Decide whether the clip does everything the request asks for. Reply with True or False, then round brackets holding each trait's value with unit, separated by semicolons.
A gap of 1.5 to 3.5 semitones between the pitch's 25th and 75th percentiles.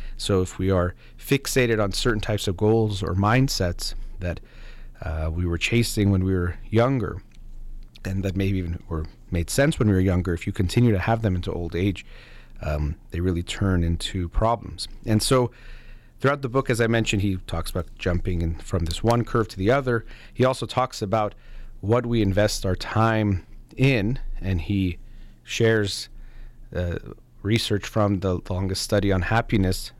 False (4.4 semitones)